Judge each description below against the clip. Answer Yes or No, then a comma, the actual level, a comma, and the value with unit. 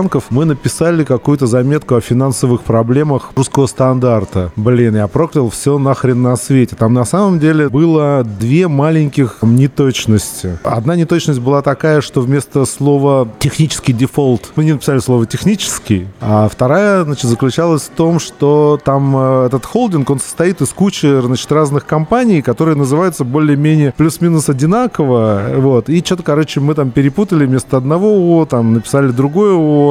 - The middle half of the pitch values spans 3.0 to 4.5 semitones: Yes, average, 3.7 semitones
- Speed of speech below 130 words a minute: No, average, 145 wpm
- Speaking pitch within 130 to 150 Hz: Yes, medium, 140 Hz